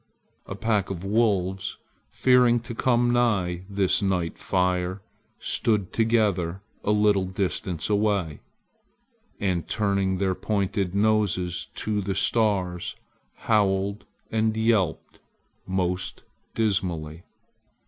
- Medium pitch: No, low, 100 Hz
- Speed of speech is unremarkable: No, slow, 100 wpm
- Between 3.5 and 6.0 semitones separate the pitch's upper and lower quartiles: No, average, 2.8 semitones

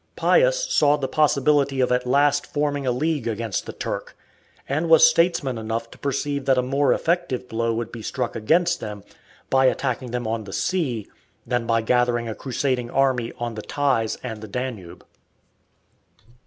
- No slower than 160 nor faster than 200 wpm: Yes, average, 170 wpm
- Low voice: Yes, low, 130 Hz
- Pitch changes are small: No, average, 3.7 semitones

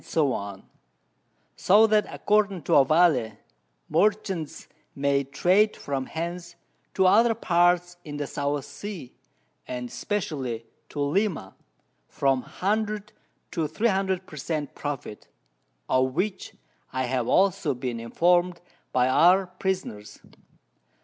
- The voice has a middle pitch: Yes, medium, 165 Hz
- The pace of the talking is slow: Yes, slow, 110 wpm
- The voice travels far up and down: Yes, wide, 6.1 semitones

